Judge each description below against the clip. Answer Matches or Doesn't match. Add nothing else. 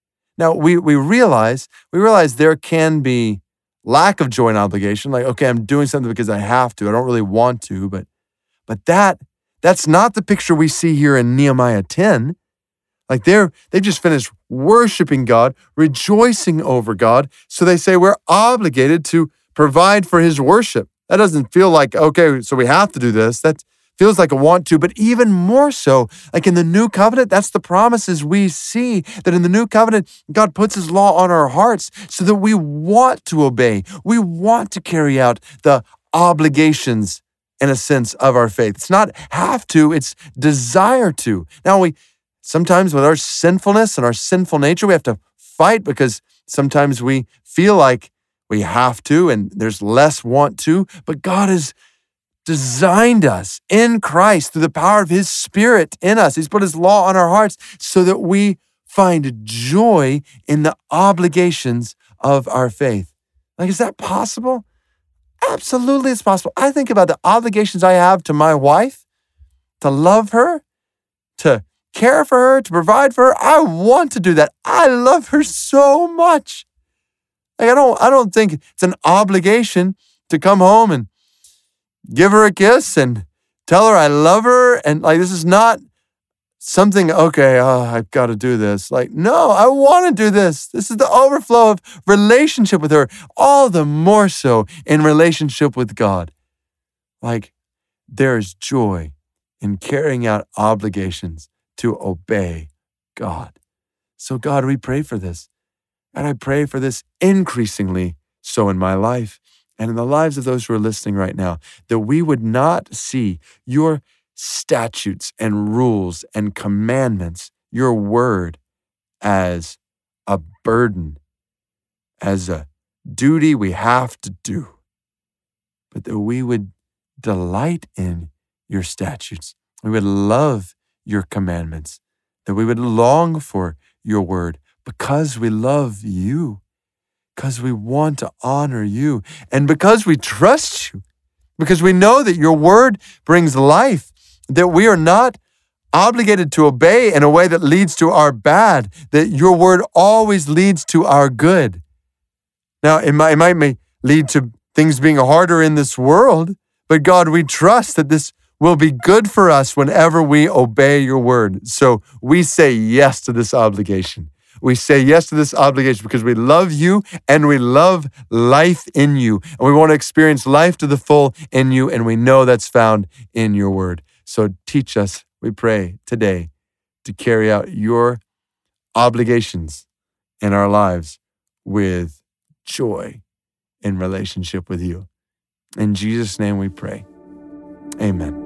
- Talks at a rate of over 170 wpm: Doesn't match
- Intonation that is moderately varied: Doesn't match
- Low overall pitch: Doesn't match